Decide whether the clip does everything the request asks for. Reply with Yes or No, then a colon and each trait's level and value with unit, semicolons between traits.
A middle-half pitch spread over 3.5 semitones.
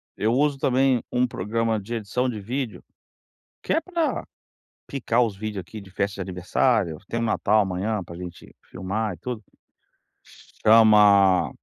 Yes: average, 3.9 semitones